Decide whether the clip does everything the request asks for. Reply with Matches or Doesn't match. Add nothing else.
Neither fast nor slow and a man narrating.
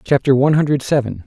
Matches